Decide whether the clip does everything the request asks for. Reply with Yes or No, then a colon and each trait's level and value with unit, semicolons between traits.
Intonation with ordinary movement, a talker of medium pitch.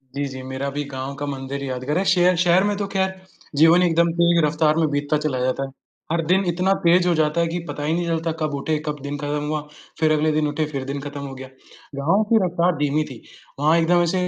Yes: average, 3.2 semitones; medium, 155 Hz